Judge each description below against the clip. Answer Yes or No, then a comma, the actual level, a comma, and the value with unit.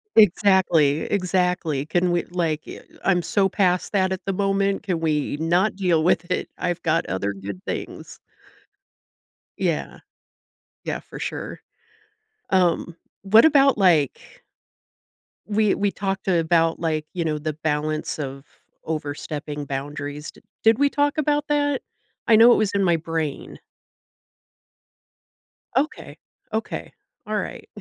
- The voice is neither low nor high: Yes, medium, 175 Hz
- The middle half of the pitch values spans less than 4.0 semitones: No, average, 4.3 semitones